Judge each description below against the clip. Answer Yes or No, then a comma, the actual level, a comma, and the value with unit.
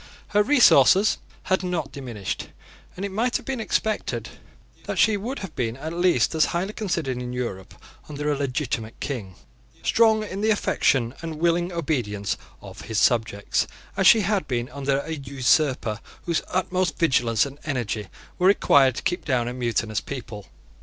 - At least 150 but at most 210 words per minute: Yes, average, 165 wpm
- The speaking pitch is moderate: Yes, medium, 145 Hz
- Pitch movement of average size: No, wide, 7.2 semitones